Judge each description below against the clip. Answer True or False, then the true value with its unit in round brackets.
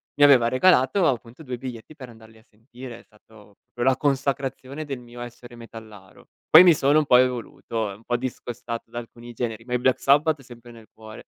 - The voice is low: True (120 Hz)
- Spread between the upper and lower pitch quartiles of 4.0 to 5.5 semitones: False (2.6 semitones)